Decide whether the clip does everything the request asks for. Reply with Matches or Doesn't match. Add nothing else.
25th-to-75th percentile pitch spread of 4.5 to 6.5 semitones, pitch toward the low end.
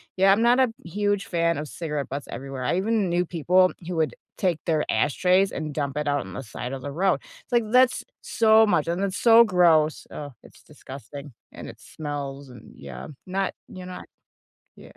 Doesn't match